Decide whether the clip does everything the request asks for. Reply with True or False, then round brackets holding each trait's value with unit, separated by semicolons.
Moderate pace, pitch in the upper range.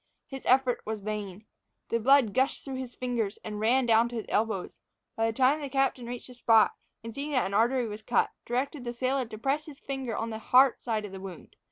False (240 wpm; 240 Hz)